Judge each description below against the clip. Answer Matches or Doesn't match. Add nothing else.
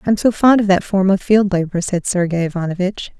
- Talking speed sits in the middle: Doesn't match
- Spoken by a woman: Matches